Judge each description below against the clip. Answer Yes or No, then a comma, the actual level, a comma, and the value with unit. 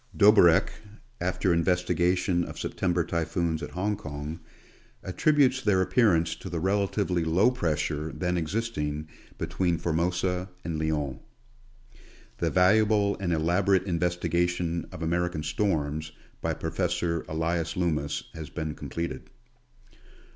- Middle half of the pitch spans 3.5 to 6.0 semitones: No, narrow, 2.5 semitones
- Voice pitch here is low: Yes, very low, 85 Hz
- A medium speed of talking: No, slow, 110 wpm